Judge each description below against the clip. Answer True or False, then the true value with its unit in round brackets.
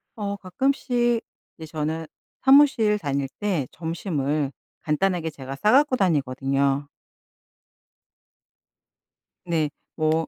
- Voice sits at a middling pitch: True (165 Hz)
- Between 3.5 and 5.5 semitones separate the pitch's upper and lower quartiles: False (6.3 semitones)